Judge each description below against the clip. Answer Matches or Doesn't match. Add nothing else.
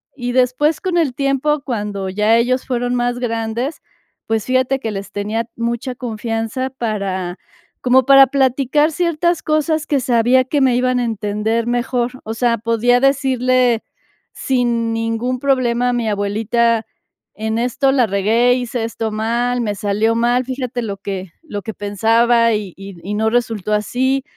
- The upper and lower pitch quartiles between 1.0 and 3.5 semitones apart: Matches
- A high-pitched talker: Matches